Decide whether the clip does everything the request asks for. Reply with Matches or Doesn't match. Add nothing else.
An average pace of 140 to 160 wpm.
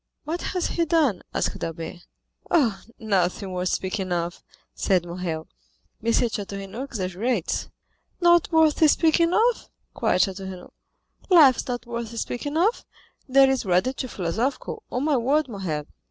Matches